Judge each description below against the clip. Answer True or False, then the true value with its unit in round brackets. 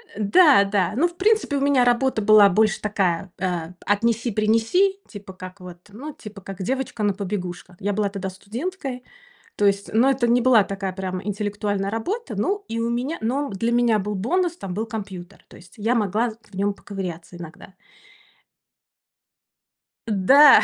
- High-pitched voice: True (210 Hz)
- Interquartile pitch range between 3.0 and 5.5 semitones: True (4.2 semitones)